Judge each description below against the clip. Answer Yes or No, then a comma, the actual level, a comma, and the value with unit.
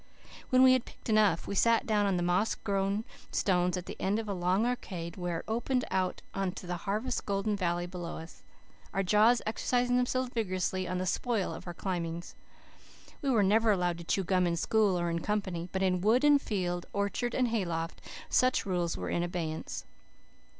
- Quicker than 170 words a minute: Yes, average, 195 wpm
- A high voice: Yes, high, 195 Hz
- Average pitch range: Yes, average, 3.9 semitones